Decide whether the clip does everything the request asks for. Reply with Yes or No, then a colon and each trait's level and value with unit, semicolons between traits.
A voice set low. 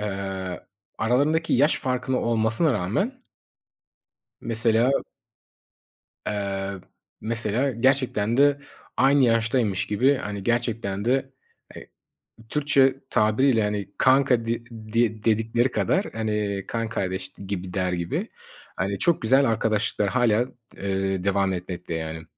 Yes: low, 110 Hz